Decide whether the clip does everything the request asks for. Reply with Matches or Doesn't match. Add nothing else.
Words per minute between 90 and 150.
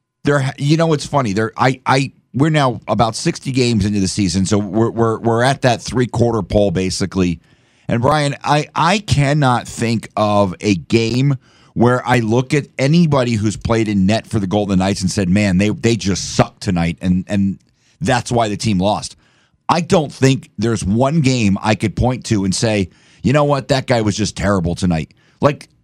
Doesn't match